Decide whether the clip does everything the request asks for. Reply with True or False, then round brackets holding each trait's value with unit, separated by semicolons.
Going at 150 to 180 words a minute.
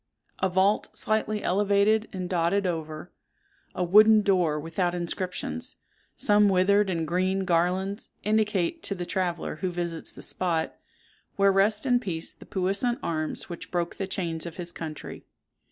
False (140 wpm)